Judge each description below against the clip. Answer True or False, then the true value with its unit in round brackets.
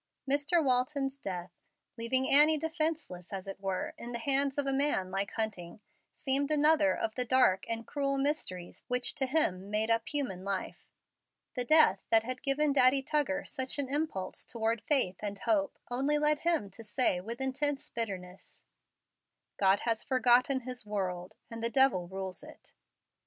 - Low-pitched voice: False (255 Hz)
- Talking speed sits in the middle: True (165 wpm)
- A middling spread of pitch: False (6.1 semitones)